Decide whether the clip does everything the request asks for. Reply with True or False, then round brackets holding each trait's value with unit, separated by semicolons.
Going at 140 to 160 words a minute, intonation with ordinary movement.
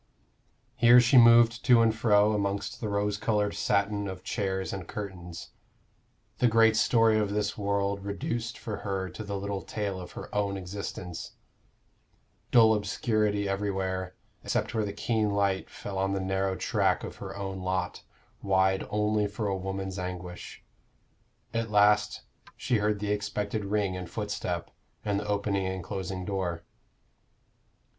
False (150 wpm; 1.8 semitones)